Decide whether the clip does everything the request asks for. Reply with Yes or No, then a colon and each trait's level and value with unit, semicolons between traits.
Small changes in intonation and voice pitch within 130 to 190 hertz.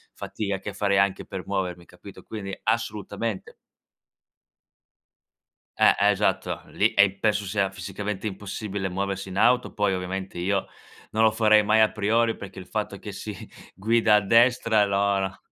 No: narrow, 2.0 semitones; low, 100 Hz